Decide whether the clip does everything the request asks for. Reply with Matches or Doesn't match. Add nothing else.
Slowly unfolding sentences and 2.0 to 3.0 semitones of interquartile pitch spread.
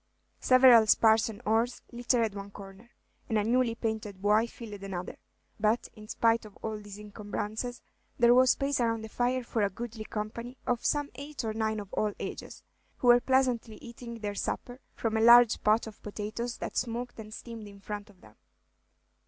Doesn't match